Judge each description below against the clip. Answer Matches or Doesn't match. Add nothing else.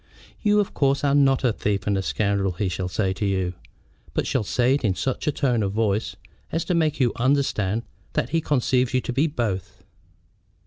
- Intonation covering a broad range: Matches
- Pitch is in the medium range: Doesn't match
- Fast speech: Matches